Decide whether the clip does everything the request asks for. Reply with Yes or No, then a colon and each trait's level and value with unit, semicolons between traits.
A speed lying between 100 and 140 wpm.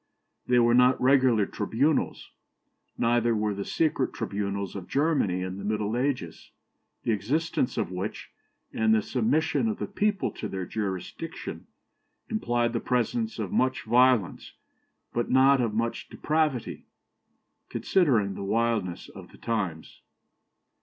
Yes: slow, 135 wpm